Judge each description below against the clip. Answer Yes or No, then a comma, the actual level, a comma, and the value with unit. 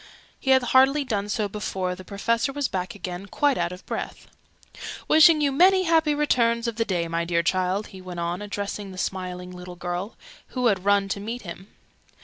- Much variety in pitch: Yes, wide, 5.7 semitones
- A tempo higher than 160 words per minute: Yes, average, 195 wpm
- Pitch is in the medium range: No, high, 205 Hz